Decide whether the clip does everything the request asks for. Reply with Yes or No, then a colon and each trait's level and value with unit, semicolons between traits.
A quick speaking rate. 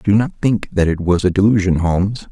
Yes: fast, 235 wpm